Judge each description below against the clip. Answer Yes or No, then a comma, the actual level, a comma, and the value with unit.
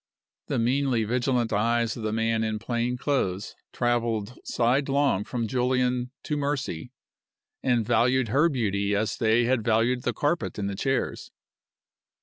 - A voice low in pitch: Yes, low, 120 Hz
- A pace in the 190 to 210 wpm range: No, average, 140 wpm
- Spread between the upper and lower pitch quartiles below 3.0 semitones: Yes, narrow, 2.5 semitones